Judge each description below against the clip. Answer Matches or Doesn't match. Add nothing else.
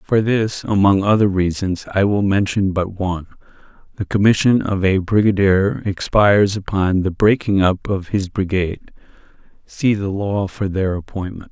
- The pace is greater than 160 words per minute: Doesn't match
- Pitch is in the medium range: Doesn't match